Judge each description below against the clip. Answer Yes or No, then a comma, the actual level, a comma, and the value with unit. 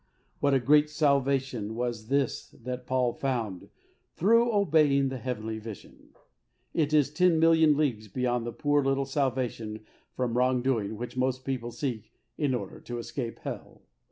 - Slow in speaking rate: No, average, 155 wpm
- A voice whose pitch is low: Yes, low, 130 Hz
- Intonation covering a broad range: No, average, 3.3 semitones